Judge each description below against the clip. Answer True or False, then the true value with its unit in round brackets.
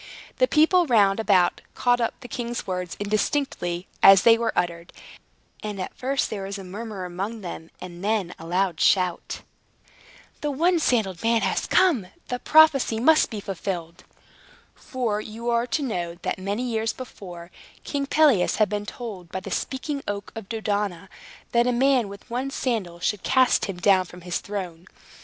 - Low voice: False (210 Hz)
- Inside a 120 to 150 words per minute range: False (170 wpm)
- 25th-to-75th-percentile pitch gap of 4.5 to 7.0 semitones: True (5.0 semitones)